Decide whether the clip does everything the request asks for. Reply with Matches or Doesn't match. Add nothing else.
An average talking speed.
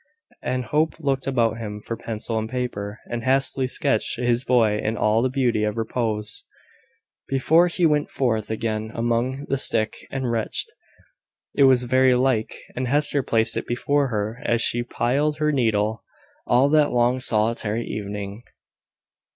Matches